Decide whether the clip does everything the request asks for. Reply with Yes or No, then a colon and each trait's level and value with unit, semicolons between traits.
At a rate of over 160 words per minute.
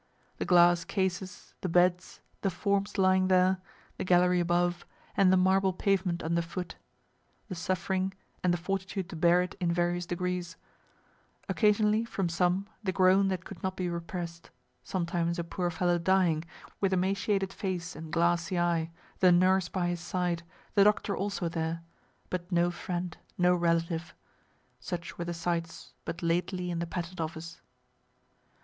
No: average, 155 wpm